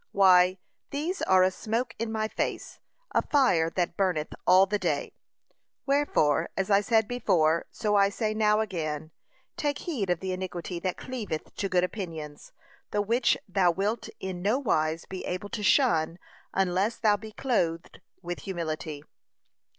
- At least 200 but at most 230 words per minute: No, average, 155 wpm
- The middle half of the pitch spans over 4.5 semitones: No, average, 4.0 semitones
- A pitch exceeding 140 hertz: Yes, high, 190 Hz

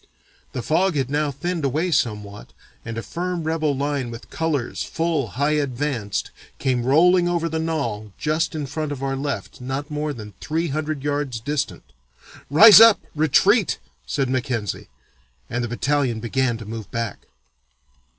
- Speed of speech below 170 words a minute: Yes, average, 155 wpm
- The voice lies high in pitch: No, medium, 145 Hz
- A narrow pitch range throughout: No, average, 4.6 semitones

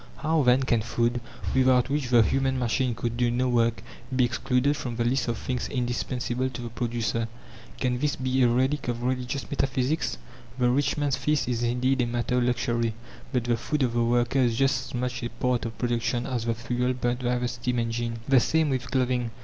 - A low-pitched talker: Yes, low, 125 Hz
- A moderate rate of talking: No, fast, 210 wpm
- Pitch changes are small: Yes, narrow, 1.5 semitones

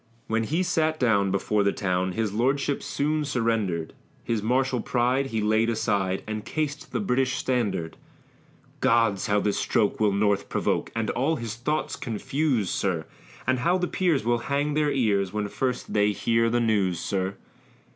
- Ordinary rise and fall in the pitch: Yes, average, 4.6 semitones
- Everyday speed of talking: Yes, average, 165 wpm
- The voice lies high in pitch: No, low, 115 Hz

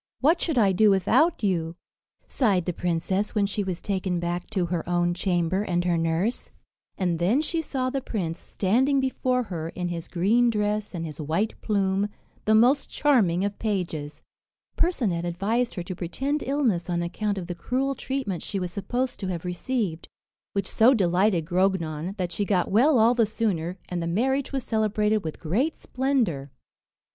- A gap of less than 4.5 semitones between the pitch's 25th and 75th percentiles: No, average, 5.3 semitones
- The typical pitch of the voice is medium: No, high, 195 Hz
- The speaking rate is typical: Yes, average, 175 wpm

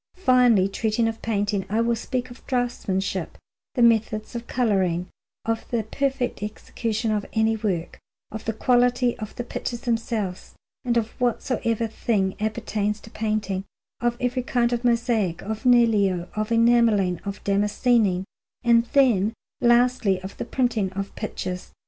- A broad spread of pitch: No, average, 2.8 semitones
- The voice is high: Yes, high, 225 Hz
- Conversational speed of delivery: Yes, average, 150 wpm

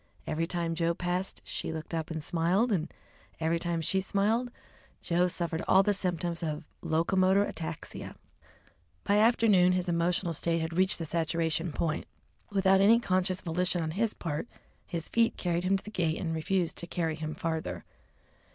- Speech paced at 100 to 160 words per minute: No, average, 170 wpm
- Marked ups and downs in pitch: No, narrow, 2.6 semitones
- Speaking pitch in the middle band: Yes, medium, 175 Hz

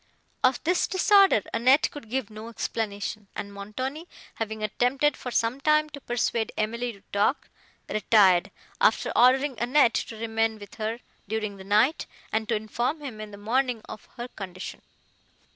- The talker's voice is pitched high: Yes, high, 230 Hz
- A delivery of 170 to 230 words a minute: No, average, 160 wpm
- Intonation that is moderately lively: Yes, average, 3.6 semitones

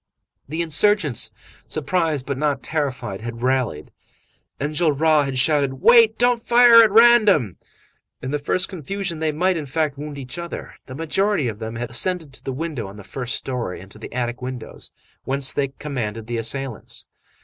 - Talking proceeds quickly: No, average, 170 wpm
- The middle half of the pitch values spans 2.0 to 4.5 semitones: No, average, 5.1 semitones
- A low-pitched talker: No, medium, 145 Hz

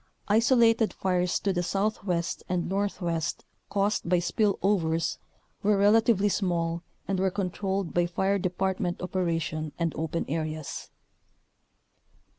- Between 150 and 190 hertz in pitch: Yes, medium, 185 Hz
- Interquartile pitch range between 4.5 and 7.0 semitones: No, average, 2.8 semitones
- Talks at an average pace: No, slow, 115 wpm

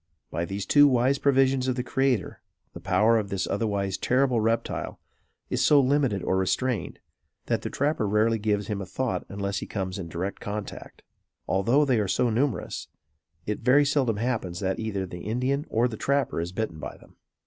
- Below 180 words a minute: No, average, 185 wpm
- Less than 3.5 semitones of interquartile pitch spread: No, average, 4.9 semitones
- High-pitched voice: No, low, 110 Hz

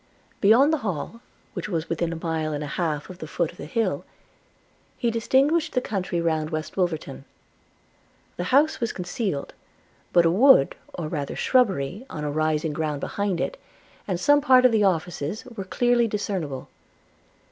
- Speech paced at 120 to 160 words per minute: No, average, 170 wpm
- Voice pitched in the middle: Yes, medium, 180 Hz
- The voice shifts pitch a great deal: Yes, wide, 6.8 semitones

